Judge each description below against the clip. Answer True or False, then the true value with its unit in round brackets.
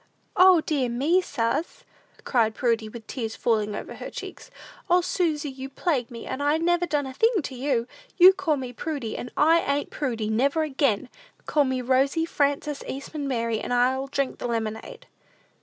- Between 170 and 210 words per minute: True (175 wpm)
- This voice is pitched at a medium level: False (275 Hz)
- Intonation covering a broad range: False (4.6 semitones)